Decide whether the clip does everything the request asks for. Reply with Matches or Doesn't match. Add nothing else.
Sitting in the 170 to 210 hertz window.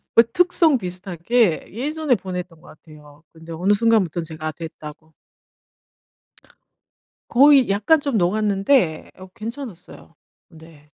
Matches